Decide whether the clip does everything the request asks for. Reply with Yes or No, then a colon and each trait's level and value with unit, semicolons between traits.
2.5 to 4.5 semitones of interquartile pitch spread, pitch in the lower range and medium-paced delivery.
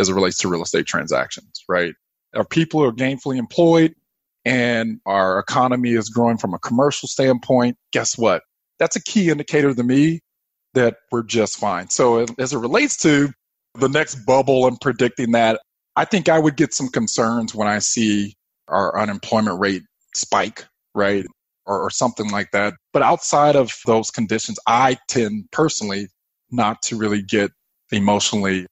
No: average, 5.1 semitones; low, 120 Hz; average, 165 wpm